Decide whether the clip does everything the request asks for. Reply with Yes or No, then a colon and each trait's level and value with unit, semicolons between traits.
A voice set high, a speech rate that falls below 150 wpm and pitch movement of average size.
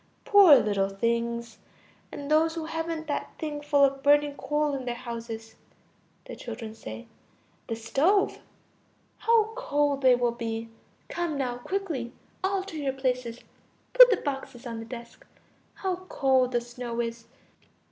Yes: very high, 265 Hz; average, 140 wpm; average, 5.0 semitones